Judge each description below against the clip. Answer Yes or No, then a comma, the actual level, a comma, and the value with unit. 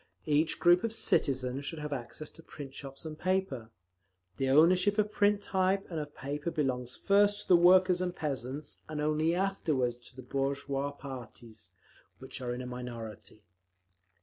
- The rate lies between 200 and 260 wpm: No, average, 165 wpm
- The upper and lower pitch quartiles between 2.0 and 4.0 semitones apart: No, wide, 5.5 semitones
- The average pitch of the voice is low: No, medium, 145 Hz